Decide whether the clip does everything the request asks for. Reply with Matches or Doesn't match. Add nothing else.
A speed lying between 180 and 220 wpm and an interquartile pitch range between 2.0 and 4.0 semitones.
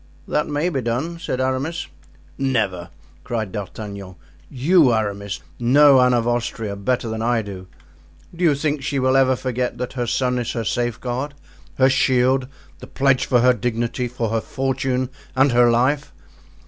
Doesn't match